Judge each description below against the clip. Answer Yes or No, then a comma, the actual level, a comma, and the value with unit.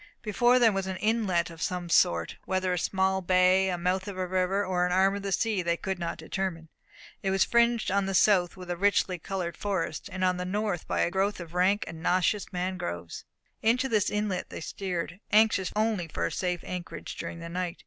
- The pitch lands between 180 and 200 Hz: Yes, medium, 185 Hz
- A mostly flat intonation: Yes, narrow, 2.1 semitones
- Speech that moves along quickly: Yes, fast, 215 wpm